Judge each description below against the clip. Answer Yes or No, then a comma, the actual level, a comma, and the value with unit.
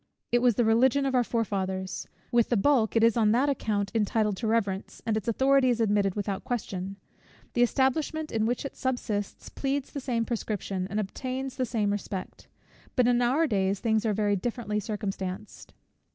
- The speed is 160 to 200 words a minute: Yes, average, 180 wpm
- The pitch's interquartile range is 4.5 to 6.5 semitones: No, average, 3.4 semitones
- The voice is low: No, high, 225 Hz